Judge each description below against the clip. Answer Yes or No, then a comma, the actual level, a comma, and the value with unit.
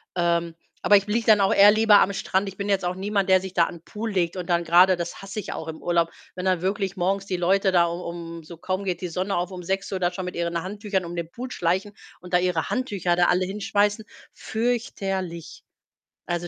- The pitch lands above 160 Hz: Yes, medium, 185 Hz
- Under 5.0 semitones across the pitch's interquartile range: Yes, narrow, 2.5 semitones